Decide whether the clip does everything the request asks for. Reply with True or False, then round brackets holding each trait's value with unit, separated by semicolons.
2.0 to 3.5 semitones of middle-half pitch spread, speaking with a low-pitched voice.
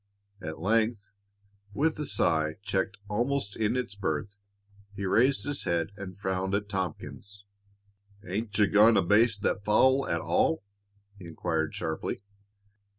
True (3.2 semitones; 100 Hz)